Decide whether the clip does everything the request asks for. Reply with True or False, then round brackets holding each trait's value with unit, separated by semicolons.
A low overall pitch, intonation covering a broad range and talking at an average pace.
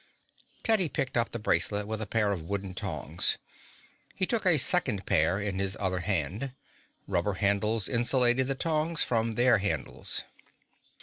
False (110 Hz; 4.9 semitones; 150 wpm)